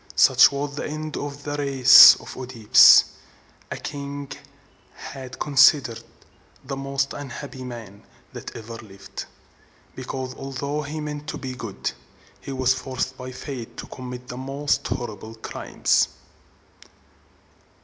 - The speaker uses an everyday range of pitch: No, narrow, 2.2 semitones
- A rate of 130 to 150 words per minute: Yes, slow, 135 wpm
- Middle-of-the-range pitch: No, low, 130 Hz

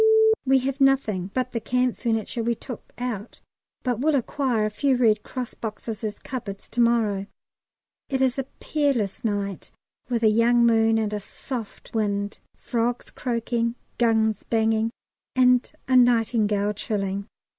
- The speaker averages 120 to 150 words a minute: Yes, average, 145 wpm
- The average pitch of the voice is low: No, high, 230 Hz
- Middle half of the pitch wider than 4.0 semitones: No, average, 2.8 semitones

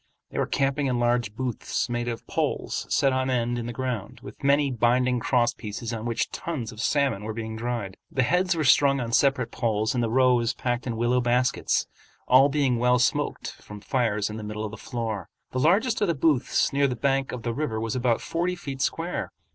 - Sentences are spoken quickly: Yes, fast, 215 wpm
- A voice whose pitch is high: No, low, 125 Hz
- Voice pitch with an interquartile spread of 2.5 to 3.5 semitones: Yes, average, 2.9 semitones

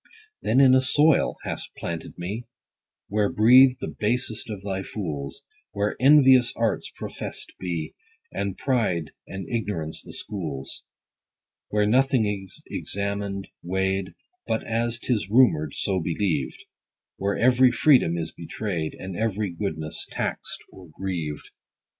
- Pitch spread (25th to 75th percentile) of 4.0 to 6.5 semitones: Yes, average, 5.1 semitones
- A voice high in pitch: No, low, 100 Hz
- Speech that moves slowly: Yes, slow, 130 wpm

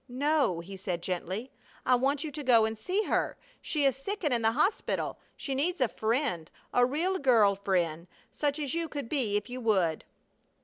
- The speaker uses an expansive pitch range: Yes, wide, 6.4 semitones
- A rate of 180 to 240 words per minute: Yes, average, 195 wpm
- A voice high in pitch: Yes, very high, 250 Hz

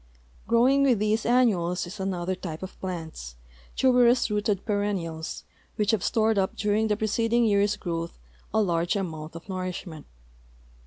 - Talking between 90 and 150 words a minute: Yes, average, 145 wpm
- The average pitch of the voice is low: No, high, 200 Hz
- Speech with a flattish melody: No, average, 4.1 semitones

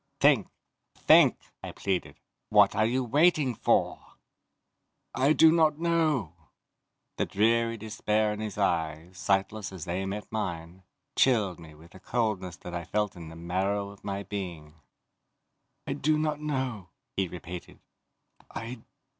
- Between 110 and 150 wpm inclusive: Yes, average, 140 wpm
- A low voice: Yes, low, 100 Hz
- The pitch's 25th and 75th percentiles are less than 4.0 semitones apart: No, wide, 5.5 semitones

